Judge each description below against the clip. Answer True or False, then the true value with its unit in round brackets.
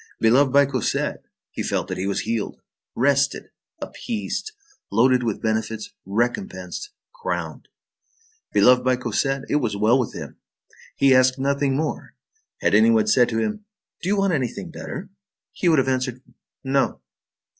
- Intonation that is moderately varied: True (4.1 semitones)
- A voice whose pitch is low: True (130 Hz)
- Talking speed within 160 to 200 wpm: False (150 wpm)